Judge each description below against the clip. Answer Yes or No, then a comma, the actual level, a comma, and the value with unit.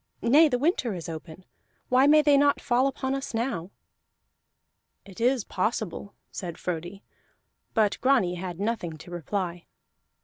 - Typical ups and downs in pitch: No, wide, 6.9 semitones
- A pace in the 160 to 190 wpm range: No, average, 140 wpm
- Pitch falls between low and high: No, high, 215 Hz